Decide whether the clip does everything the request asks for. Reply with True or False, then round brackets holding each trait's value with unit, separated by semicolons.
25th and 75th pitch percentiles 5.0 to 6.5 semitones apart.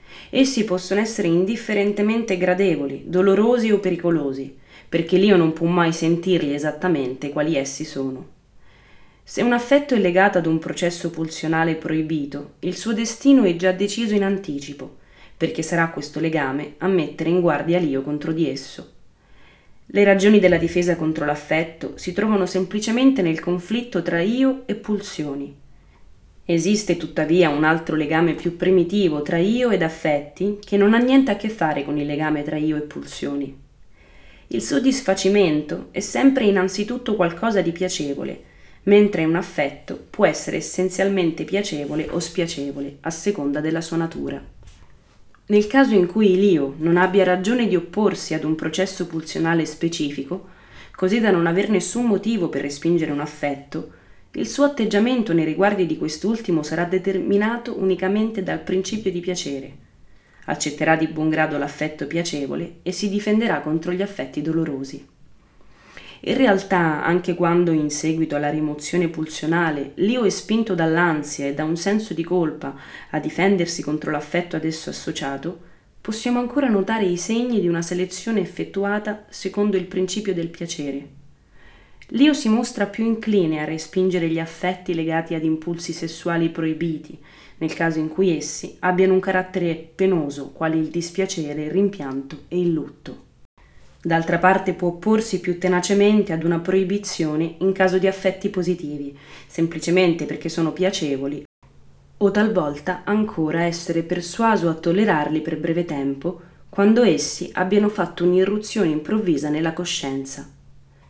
False (3.9 semitones)